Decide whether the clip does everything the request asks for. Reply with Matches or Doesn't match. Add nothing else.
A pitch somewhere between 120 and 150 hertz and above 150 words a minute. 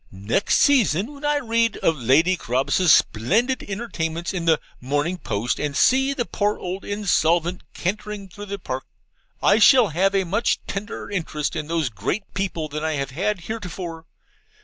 Doesn't match